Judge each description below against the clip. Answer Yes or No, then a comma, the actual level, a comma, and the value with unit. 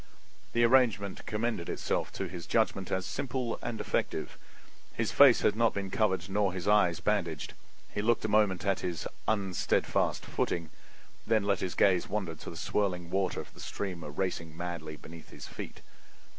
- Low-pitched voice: Yes, very low, 95 Hz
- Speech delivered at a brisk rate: No, average, 170 wpm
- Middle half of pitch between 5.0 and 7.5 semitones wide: No, average, 3.4 semitones